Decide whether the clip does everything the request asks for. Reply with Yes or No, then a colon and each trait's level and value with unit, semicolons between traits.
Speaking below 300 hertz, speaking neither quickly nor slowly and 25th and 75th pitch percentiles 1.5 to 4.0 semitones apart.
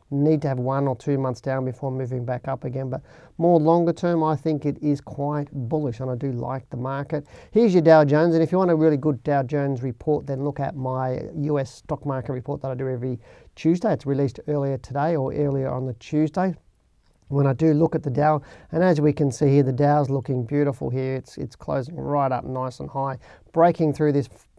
No: medium, 140 Hz; fast, 230 wpm; average, 2.8 semitones